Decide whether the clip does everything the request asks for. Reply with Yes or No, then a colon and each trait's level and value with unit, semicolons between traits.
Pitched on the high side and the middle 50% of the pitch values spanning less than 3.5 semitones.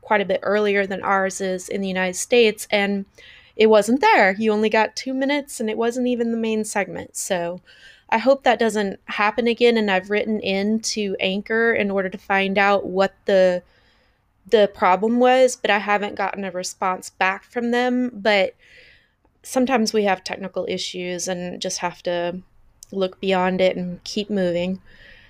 Yes: high, 200 Hz; average, 3.1 semitones